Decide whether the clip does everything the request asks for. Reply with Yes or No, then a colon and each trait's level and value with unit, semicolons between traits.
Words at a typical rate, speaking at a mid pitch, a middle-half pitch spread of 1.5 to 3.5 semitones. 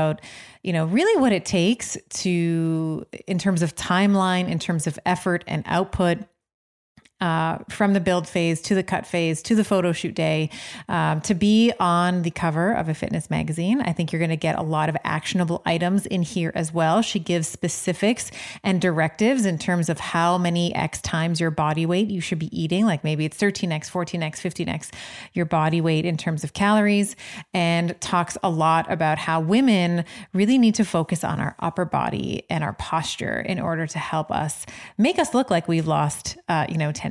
Yes: average, 195 wpm; medium, 175 Hz; average, 2.8 semitones